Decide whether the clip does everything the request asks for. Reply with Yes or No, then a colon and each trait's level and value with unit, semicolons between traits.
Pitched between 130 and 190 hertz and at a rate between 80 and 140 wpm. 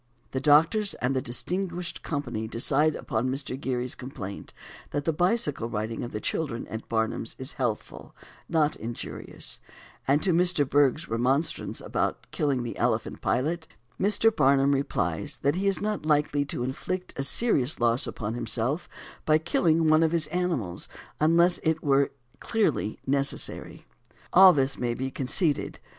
No: medium, 140 Hz; average, 150 wpm